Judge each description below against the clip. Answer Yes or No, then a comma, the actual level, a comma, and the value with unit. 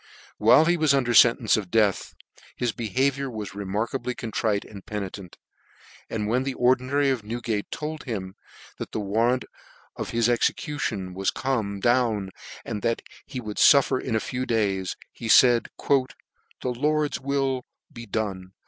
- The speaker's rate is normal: Yes, average, 155 wpm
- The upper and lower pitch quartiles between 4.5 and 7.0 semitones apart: No, average, 3.9 semitones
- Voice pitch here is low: Yes, low, 115 Hz